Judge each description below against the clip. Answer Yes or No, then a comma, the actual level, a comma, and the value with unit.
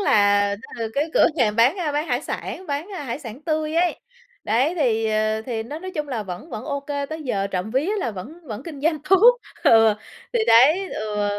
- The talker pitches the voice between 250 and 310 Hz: Yes, very high, 260 Hz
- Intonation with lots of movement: Yes, wide, 6.4 semitones